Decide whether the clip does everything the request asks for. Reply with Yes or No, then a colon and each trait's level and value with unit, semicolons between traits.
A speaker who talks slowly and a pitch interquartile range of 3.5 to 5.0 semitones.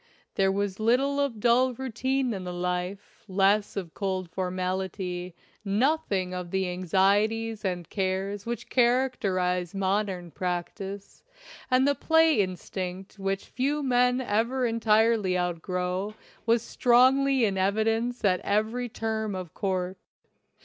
Yes: slow, 125 wpm; average, 4.4 semitones